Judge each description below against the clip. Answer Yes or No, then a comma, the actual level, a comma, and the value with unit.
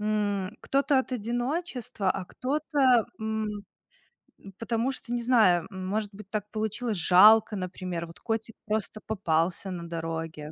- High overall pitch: Yes, high, 215 Hz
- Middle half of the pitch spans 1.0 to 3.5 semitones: No, average, 4.1 semitones